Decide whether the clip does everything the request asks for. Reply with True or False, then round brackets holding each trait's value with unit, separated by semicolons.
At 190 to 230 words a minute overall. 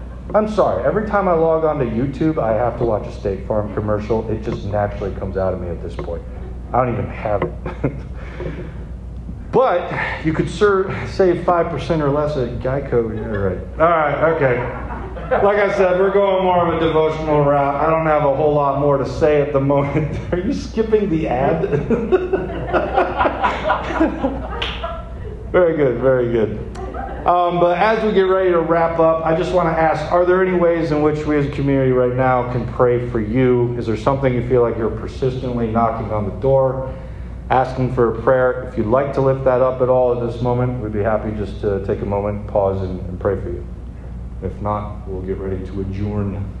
True (200 wpm)